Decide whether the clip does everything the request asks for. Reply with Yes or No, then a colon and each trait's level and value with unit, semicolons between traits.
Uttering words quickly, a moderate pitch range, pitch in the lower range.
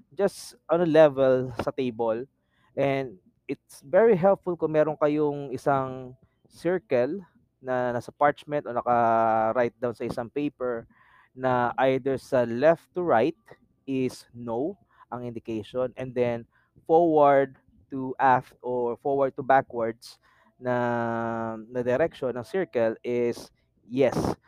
No: average, 125 wpm; average, 3.4 semitones; low, 130 Hz